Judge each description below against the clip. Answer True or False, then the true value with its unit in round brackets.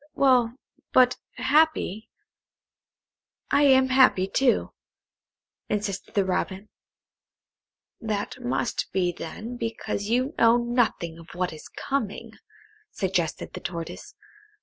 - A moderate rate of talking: False (105 wpm)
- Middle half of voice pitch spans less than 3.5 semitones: False (5.0 semitones)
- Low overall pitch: False (225 Hz)